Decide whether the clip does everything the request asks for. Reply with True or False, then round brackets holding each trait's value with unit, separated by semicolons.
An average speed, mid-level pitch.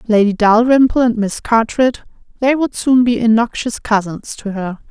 False (145 wpm; 230 Hz)